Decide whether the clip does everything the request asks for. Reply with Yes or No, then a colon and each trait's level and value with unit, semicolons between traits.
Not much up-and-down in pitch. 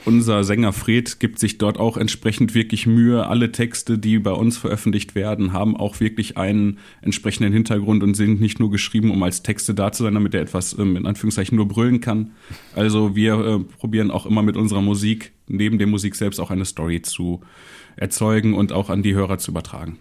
Yes: narrow, 1.8 semitones